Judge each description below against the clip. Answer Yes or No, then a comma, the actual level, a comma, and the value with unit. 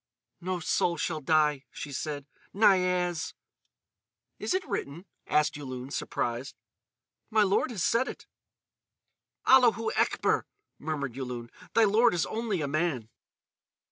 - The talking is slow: Yes, slow, 120 wpm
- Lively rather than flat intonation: Yes, wide, 6.5 semitones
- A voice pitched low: No, medium, 165 Hz